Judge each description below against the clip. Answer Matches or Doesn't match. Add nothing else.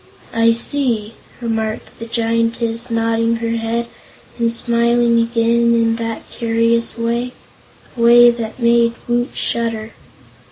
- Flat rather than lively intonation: Matches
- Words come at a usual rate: Doesn't match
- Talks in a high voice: Matches